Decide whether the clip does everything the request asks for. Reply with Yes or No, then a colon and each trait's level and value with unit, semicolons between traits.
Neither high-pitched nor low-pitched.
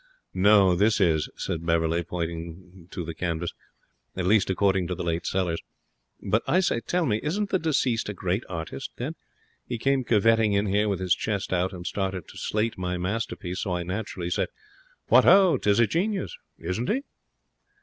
No: very low, 95 Hz